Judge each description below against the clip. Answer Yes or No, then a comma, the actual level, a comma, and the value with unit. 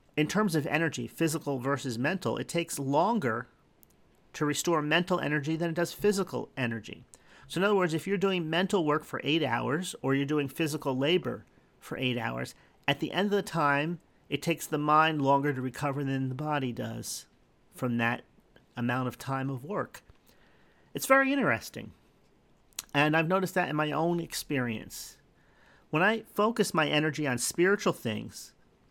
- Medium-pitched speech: Yes, medium, 150 Hz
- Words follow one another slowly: No, average, 170 wpm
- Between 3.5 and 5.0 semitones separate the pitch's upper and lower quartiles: Yes, average, 4.1 semitones